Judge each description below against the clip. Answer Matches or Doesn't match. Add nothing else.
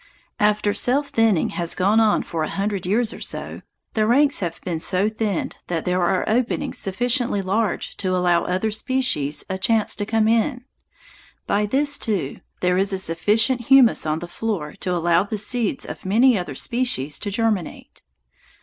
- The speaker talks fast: Doesn't match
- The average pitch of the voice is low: Doesn't match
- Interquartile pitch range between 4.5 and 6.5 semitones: Doesn't match